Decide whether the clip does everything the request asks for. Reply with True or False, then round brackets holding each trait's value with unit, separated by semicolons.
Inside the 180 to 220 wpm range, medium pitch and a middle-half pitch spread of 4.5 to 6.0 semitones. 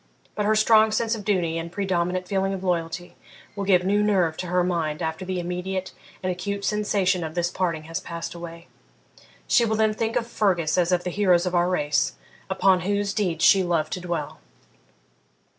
False (195 wpm; 180 Hz; 2.8 semitones)